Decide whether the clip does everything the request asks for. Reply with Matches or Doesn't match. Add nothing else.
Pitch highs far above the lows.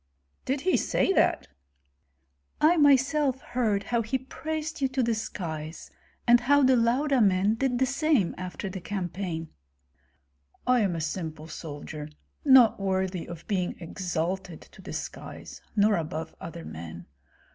Matches